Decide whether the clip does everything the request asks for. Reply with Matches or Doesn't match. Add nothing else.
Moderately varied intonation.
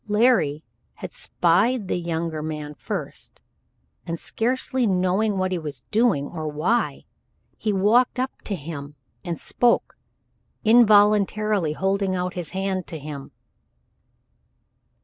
Matches